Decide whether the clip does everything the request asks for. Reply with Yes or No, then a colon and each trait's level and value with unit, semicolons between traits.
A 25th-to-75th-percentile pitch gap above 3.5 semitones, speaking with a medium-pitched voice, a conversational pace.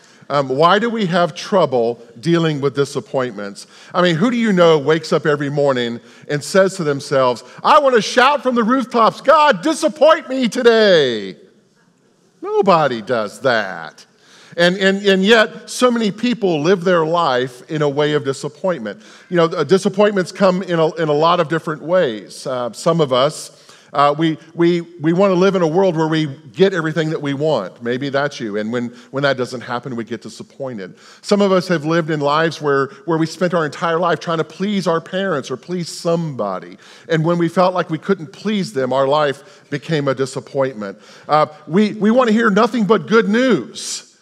Yes: wide, 5.5 semitones; medium, 165 Hz; average, 195 wpm